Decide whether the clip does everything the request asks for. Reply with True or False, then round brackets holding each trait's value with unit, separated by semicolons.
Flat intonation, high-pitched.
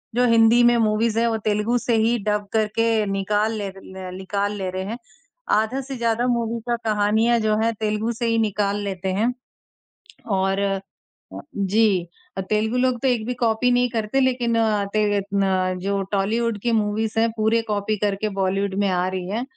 True (2.3 semitones; 220 Hz)